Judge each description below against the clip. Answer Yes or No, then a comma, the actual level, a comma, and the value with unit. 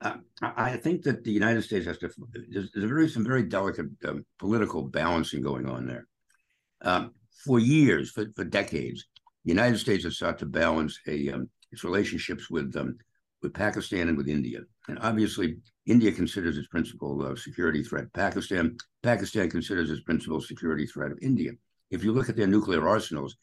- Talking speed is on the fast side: No, average, 180 wpm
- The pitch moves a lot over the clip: Yes, wide, 8.4 semitones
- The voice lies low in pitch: Yes, low, 105 Hz